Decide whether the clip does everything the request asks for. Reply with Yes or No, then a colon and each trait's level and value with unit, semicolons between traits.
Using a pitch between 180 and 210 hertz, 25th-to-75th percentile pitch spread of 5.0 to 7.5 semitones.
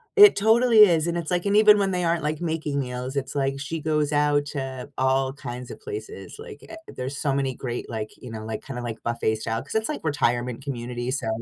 No: medium, 140 Hz; wide, 5.5 semitones